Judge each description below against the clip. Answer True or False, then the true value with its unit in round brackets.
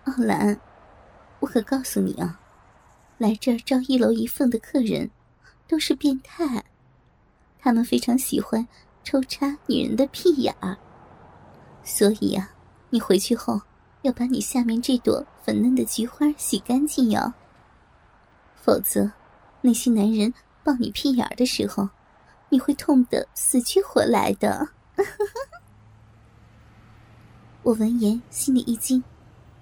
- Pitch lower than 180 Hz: False (240 Hz)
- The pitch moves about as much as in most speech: True (4.6 semitones)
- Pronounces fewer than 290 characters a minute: True (180 characters per minute)